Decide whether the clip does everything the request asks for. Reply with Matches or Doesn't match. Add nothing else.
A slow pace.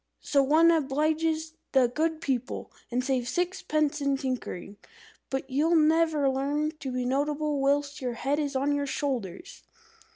Doesn't match